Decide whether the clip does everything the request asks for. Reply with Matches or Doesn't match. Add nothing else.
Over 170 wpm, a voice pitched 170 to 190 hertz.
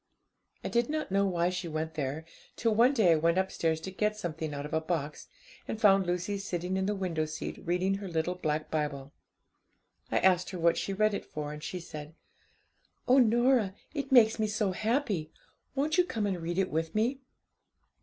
Matches